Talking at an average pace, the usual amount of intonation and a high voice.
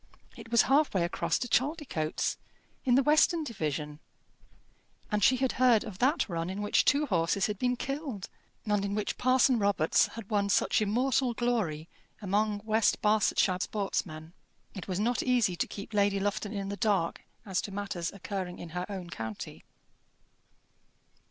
Yes: average, 165 wpm; average, 4.8 semitones; high, 205 Hz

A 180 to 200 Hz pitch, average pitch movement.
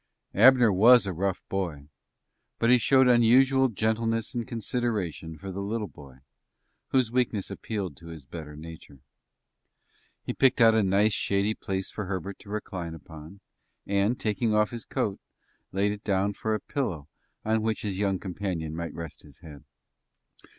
No: low, 100 Hz; average, 4.6 semitones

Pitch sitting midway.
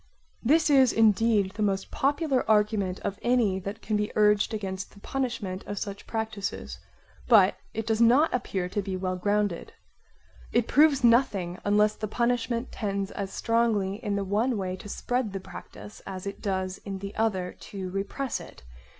No: high, 210 Hz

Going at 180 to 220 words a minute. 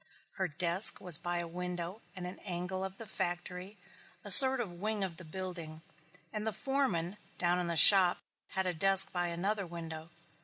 Yes: average, 185 wpm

